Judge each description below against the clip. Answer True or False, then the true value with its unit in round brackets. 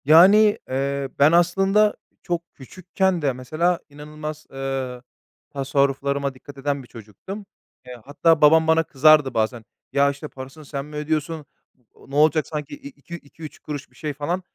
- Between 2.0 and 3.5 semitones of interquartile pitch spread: True (3.0 semitones)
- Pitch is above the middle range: False (150 Hz)